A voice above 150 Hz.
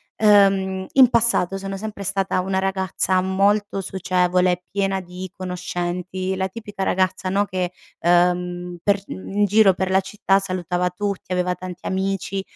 Yes: high, 190 Hz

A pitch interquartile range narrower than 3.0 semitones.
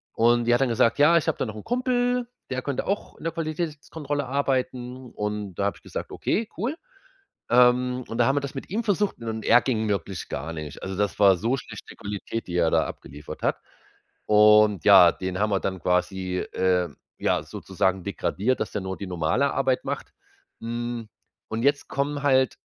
No: wide, 6.1 semitones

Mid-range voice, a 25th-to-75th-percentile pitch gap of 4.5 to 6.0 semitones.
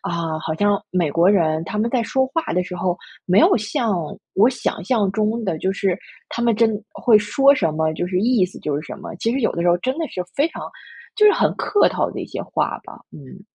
No: high, 200 Hz; average, 5.3 semitones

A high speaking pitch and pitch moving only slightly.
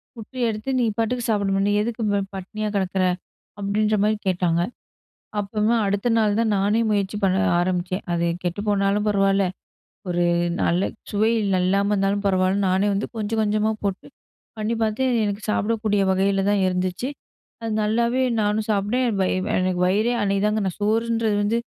Yes: high, 205 Hz; narrow, 1.9 semitones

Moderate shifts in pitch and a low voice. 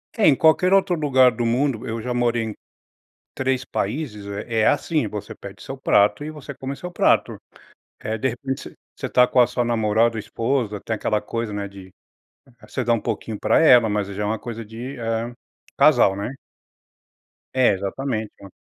Yes: average, 3.7 semitones; low, 115 Hz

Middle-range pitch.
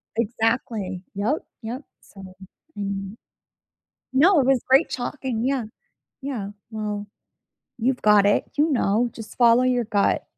No: high, 230 Hz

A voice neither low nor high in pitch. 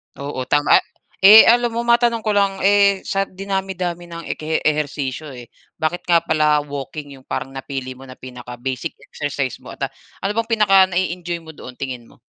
Yes: medium, 160 Hz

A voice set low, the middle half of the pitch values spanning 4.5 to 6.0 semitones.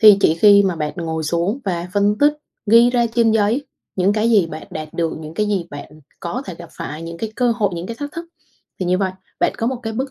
No: high, 200 Hz; average, 5.2 semitones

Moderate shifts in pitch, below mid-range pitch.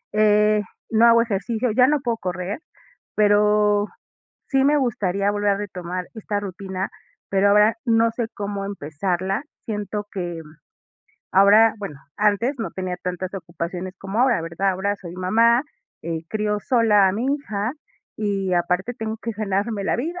No: average, 3.0 semitones; high, 205 Hz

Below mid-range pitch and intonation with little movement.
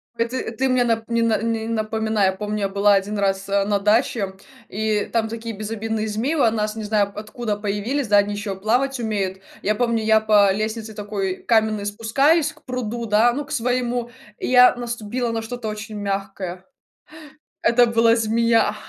No: high, 220 Hz; narrow, 2.1 semitones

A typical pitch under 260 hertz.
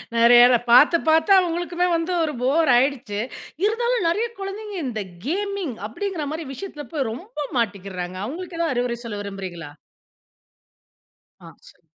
No: very high, 295 Hz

